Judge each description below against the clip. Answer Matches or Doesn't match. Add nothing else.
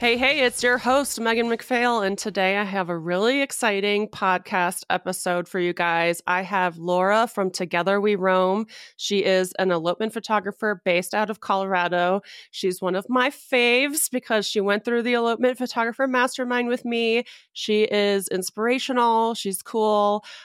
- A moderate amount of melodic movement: Matches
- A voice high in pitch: Matches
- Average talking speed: Matches